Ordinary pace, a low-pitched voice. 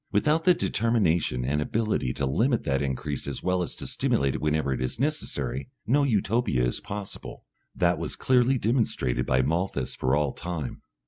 Yes: average, 175 wpm; very low, 80 Hz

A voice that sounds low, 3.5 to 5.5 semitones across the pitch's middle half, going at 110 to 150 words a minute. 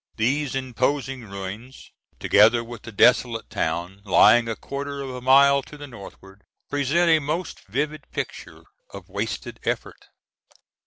Yes: low, 125 Hz; average, 4.4 semitones; average, 140 wpm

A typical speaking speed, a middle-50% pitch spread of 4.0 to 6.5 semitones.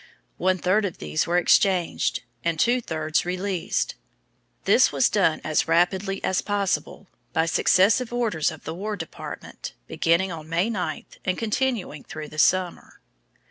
No: average, 145 wpm; average, 3.6 semitones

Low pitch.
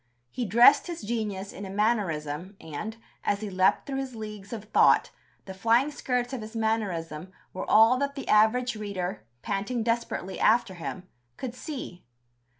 No: high, 215 Hz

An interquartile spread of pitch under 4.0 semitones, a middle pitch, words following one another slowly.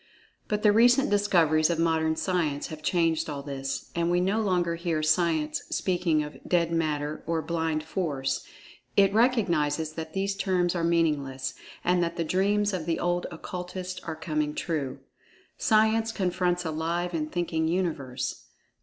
No: average, 2.8 semitones; medium, 170 Hz; average, 155 wpm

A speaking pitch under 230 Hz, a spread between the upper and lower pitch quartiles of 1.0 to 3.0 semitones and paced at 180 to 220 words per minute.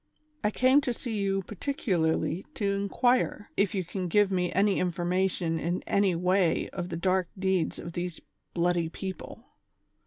No: medium, 185 Hz; narrow, 2.4 semitones; average, 155 wpm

